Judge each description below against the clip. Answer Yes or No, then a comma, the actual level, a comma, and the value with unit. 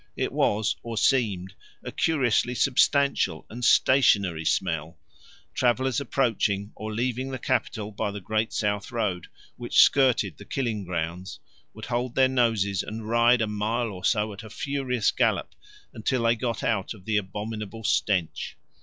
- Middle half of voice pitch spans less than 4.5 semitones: Yes, average, 3.3 semitones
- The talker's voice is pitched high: No, low, 110 Hz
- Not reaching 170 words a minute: Yes, average, 155 wpm